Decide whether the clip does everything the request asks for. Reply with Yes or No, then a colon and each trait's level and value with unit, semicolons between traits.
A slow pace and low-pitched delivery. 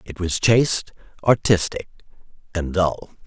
Yes: slow, 110 wpm; very low, 95 Hz